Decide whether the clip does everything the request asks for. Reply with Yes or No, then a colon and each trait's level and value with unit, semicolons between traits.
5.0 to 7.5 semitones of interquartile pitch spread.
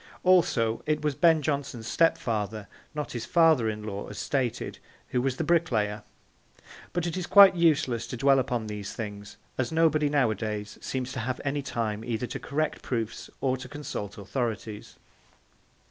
Yes: wide, 5.6 semitones